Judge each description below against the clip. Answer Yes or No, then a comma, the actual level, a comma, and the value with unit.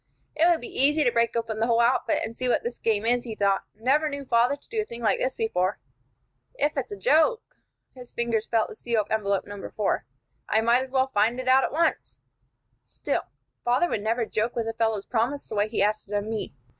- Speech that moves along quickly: Yes, fast, 235 wpm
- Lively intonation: No, average, 3.2 semitones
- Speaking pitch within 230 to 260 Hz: Yes, high, 235 Hz